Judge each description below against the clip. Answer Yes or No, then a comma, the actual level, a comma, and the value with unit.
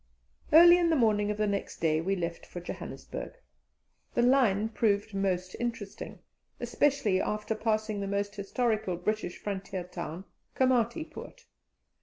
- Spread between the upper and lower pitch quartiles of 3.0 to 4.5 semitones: Yes, average, 3.5 semitones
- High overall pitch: Yes, high, 210 Hz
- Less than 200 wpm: Yes, average, 140 wpm